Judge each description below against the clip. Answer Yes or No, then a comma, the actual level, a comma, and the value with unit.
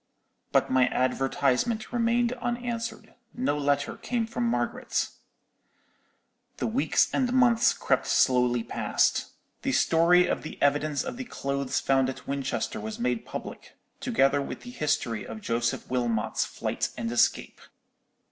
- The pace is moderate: No, slow, 130 wpm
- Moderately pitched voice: Yes, medium, 145 Hz